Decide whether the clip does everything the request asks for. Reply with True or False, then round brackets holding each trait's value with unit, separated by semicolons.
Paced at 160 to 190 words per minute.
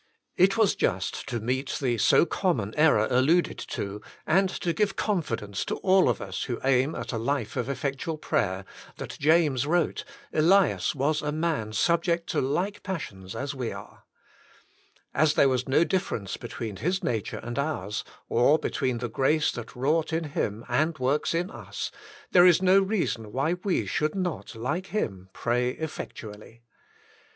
True (165 wpm)